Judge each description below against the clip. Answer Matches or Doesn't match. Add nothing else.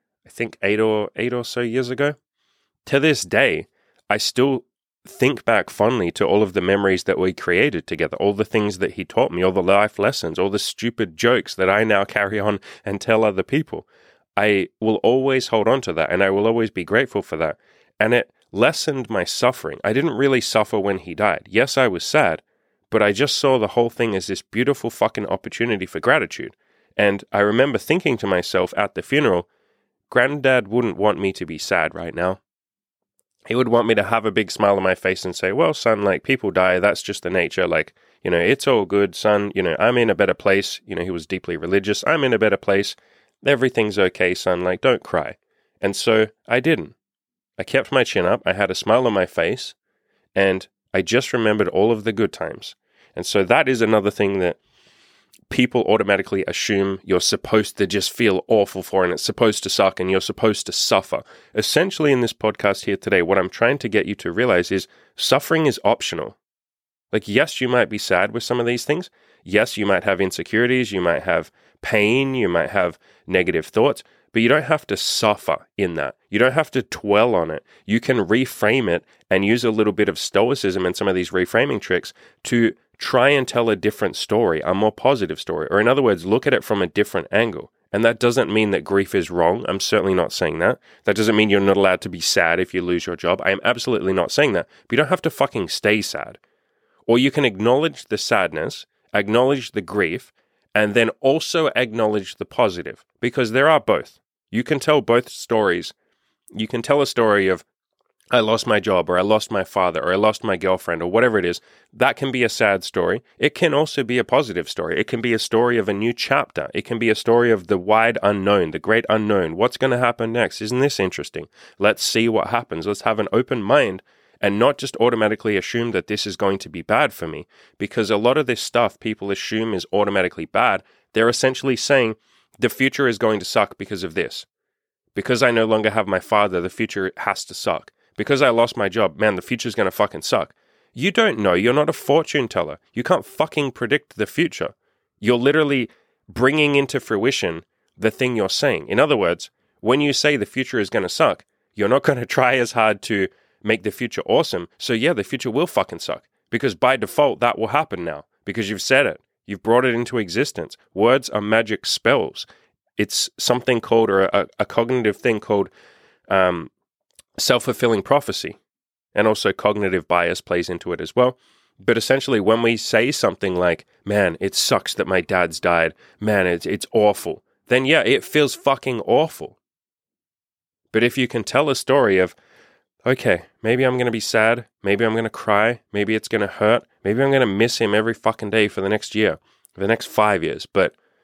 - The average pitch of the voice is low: Matches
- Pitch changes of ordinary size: Matches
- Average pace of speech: Doesn't match